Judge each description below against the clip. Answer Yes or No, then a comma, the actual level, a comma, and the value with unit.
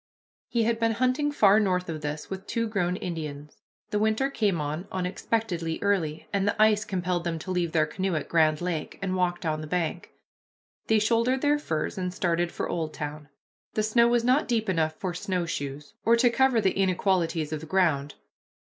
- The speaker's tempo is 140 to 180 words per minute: No, average, 190 wpm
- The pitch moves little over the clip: No, average, 5.1 semitones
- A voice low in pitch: No, medium, 185 Hz